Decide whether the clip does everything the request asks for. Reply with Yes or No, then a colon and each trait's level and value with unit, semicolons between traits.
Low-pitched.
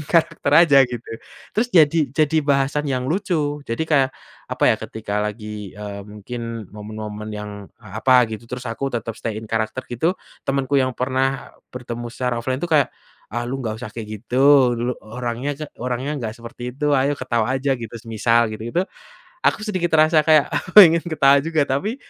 Yes: low, 130 Hz